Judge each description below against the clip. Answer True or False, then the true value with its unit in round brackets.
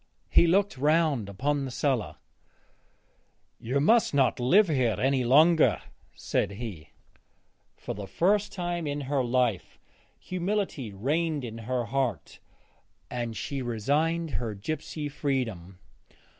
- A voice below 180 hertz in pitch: True (135 Hz)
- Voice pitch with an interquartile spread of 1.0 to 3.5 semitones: False (5.3 semitones)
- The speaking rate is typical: False (120 wpm)